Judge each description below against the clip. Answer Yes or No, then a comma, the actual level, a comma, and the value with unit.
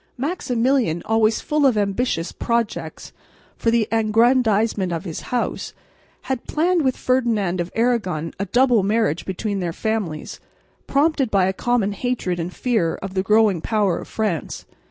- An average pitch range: Yes, average, 4.6 semitones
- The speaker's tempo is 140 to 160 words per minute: Yes, average, 150 wpm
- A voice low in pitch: No, high, 220 Hz